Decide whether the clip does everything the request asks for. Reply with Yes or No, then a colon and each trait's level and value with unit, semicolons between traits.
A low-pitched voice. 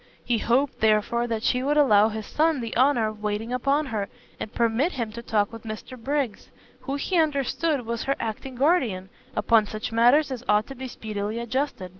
No: high, 235 Hz